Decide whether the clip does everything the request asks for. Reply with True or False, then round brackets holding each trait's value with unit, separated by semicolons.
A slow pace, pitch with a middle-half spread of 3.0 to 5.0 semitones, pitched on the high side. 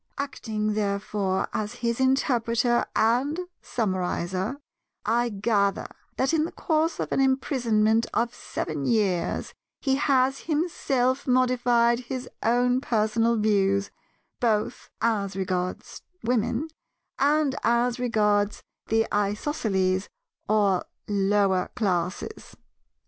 True (100 wpm; 3.8 semitones; 230 Hz)